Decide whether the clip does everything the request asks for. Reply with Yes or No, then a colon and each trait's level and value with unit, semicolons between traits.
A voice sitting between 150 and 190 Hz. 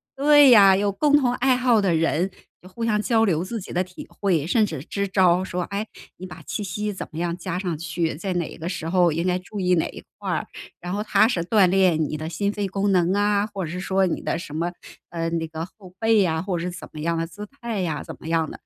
Yes: medium, 185 Hz